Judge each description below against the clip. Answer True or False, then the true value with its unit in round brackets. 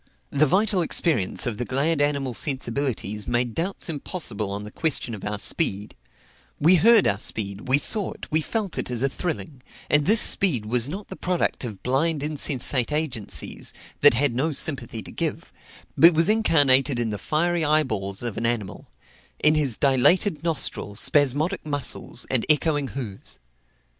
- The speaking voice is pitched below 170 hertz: True (140 Hz)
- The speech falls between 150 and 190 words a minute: True (165 wpm)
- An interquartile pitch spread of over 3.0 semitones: True (5.4 semitones)